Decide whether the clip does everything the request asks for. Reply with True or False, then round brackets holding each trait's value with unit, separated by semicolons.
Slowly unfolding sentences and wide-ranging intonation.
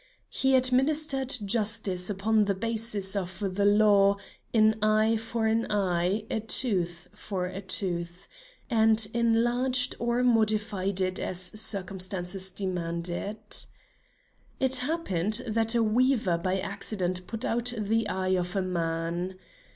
False (125 wpm; 3.5 semitones)